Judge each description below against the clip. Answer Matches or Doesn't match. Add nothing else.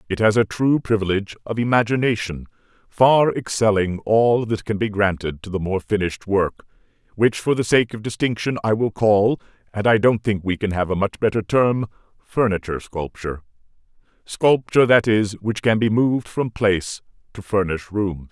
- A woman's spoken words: Doesn't match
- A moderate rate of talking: Matches